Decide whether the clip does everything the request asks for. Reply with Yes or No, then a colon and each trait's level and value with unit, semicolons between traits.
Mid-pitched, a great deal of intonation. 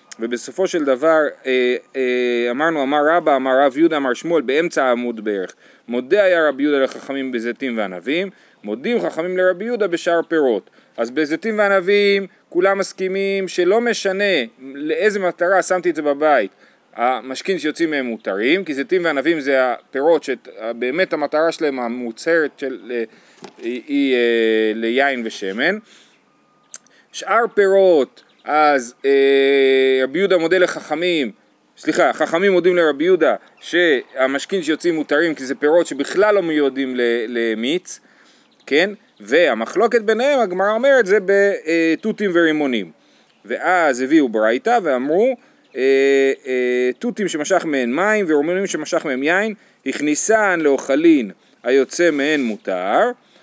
Yes: medium, 155 Hz; wide, 6.4 semitones